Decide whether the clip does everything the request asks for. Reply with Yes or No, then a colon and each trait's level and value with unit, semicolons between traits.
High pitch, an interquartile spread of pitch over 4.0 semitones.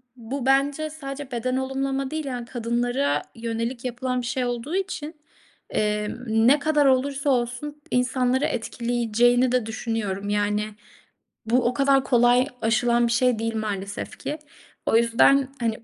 No: very high, 250 Hz; average, 2.8 semitones